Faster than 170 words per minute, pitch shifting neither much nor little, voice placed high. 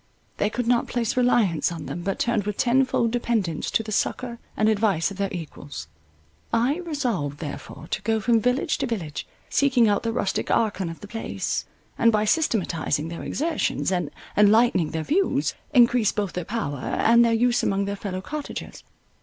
Yes: average, 180 wpm; average, 4.4 semitones; high, 215 Hz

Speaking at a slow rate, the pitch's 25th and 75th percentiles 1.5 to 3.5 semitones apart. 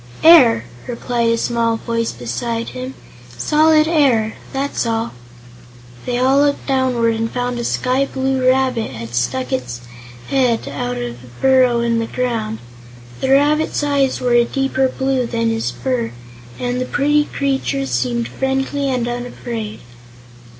No: average, 145 wpm; average, 3.1 semitones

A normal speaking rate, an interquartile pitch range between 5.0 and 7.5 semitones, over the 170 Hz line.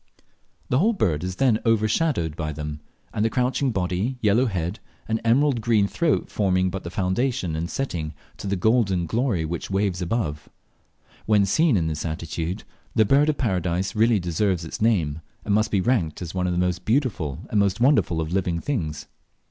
No: average, 180 wpm; average, 5.3 semitones; very low, 95 Hz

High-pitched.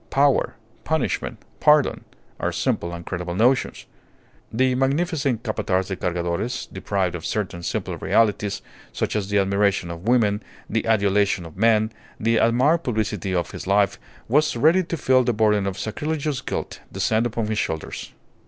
No: low, 110 Hz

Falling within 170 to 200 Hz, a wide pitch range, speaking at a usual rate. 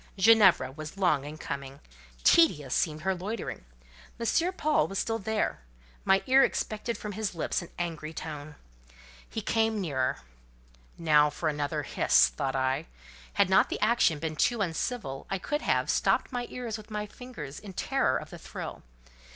Yes: medium, 185 Hz; wide, 6.6 semitones; average, 165 wpm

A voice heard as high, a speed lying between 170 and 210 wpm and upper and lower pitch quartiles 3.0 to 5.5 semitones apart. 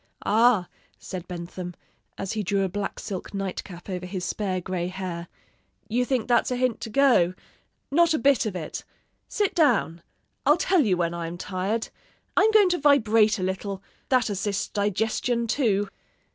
Yes: high, 205 Hz; average, 175 wpm; average, 5.1 semitones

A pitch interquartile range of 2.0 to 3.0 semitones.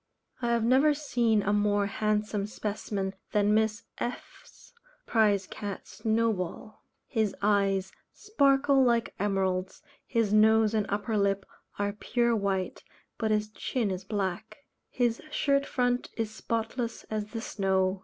Yes: narrow, 2.6 semitones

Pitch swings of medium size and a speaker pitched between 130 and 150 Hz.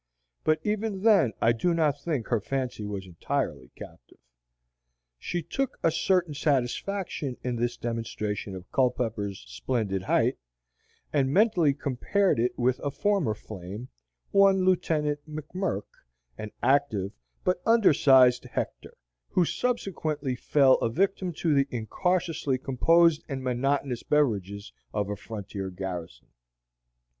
No: wide, 7.2 semitones; low, 135 Hz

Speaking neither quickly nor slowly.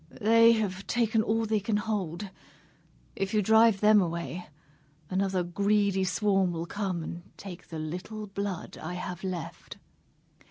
Yes: average, 145 wpm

